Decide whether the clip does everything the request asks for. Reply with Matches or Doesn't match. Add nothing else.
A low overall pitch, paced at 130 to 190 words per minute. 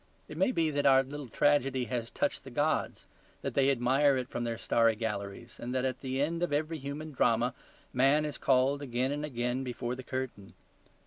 Doesn't match